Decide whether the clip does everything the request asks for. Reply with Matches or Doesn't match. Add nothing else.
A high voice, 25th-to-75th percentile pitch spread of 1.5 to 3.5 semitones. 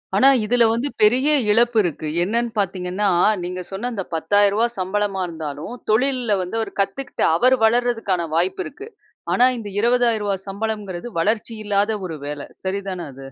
Doesn't match